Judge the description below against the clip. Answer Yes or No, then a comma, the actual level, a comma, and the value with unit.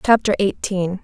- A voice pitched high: Yes, high, 195 Hz